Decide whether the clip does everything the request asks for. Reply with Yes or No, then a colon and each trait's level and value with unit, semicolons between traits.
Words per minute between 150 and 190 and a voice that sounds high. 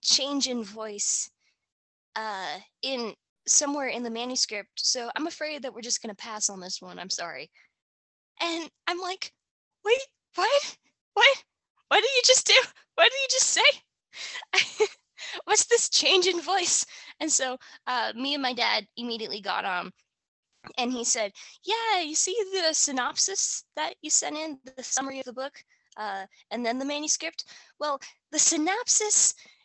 Yes: average, 160 wpm; very high, 295 Hz